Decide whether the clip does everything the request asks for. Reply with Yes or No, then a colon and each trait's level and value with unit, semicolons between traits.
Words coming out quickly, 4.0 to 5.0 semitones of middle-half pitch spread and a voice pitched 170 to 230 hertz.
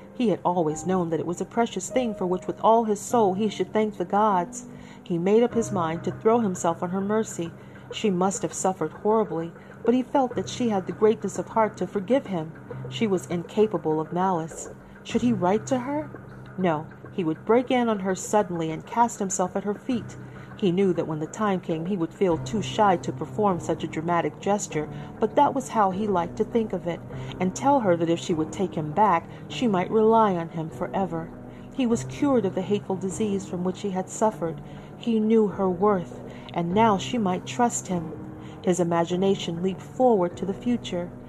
Yes: fast, 215 wpm; average, 4.3 semitones; high, 190 Hz